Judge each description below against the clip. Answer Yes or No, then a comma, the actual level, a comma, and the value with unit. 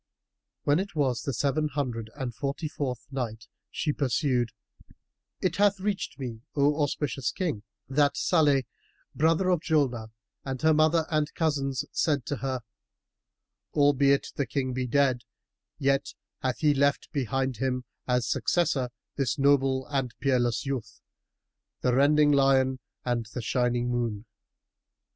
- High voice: No, low, 135 Hz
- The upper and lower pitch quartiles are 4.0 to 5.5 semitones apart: No, average, 2.8 semitones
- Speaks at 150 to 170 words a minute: No, slow, 135 wpm